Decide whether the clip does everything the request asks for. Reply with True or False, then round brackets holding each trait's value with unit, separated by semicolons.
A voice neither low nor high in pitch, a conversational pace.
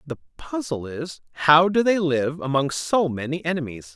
True (150 Hz; 165 wpm)